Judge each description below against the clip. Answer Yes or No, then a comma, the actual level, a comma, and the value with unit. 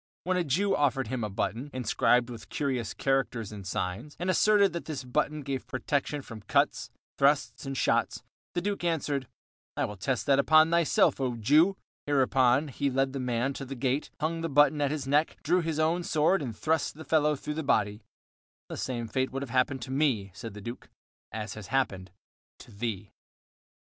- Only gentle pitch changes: No, average, 4.0 semitones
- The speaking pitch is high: No, low, 135 Hz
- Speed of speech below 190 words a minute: No, average, 195 wpm